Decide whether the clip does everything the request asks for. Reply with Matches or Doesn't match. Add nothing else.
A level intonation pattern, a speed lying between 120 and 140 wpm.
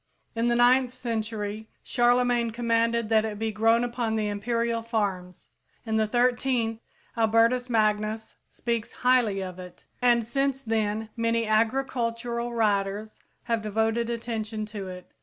Matches